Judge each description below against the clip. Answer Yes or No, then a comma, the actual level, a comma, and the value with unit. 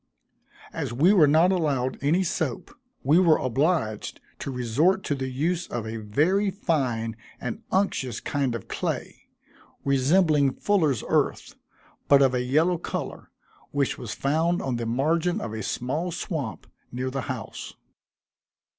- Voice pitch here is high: No, medium, 140 Hz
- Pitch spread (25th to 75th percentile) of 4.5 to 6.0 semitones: Yes, average, 5.3 semitones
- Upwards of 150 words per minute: No, average, 145 wpm